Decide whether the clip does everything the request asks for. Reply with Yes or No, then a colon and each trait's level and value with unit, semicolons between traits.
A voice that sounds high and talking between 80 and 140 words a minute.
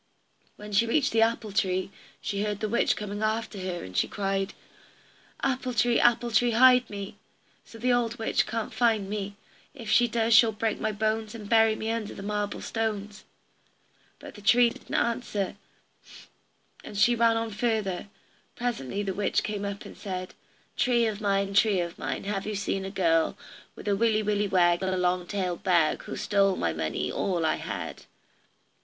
No: high, 210 Hz; average, 185 wpm